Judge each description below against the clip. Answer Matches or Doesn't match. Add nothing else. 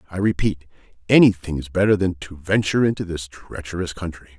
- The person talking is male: Matches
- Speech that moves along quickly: Doesn't match